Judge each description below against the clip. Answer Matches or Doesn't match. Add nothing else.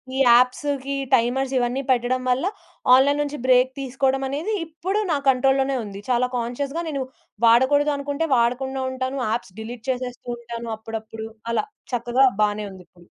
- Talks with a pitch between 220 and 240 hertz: Doesn't match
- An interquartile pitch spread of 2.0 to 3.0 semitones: Matches